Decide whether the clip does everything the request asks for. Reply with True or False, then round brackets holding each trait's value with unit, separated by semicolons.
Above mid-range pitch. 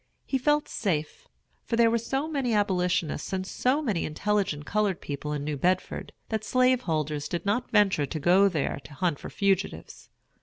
True (195 Hz)